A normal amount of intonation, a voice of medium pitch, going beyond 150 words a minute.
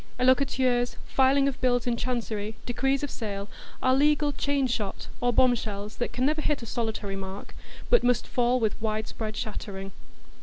No: average, 3.4 semitones; high, 245 Hz; average, 165 wpm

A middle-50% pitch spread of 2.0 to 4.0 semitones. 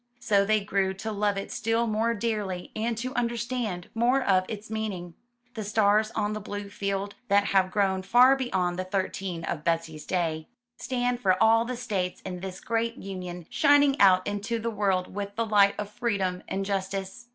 Yes: average, 3.3 semitones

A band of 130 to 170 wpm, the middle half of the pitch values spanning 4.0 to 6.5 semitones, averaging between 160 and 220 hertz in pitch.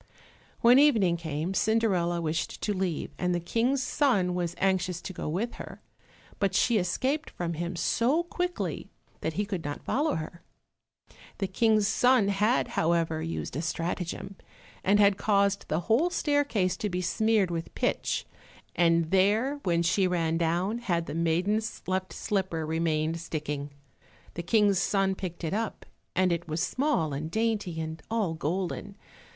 Yes: average, 155 wpm; average, 4.4 semitones; medium, 185 Hz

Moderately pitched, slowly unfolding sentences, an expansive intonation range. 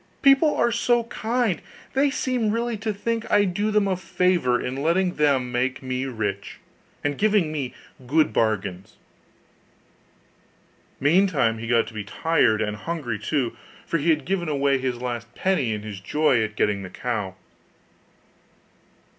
No: medium, 145 Hz; average, 155 wpm; wide, 8.8 semitones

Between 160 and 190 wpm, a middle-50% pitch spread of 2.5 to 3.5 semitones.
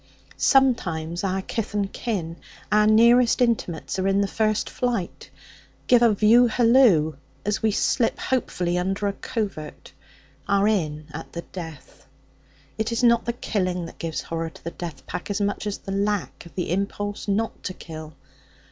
No: average, 165 wpm; average, 4.6 semitones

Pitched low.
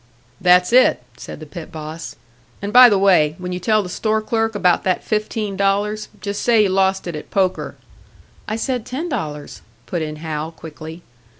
No: high, 190 Hz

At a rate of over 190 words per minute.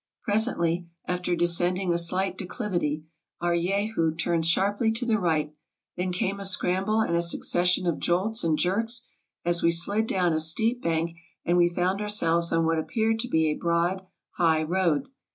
No: average, 175 wpm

